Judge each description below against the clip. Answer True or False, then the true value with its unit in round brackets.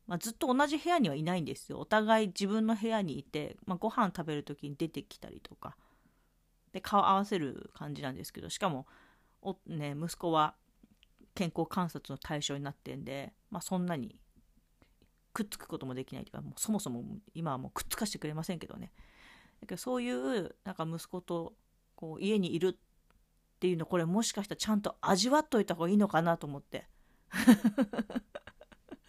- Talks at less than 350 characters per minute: False (365 characters per minute)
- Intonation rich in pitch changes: True (5.8 semitones)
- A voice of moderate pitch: True (180 Hz)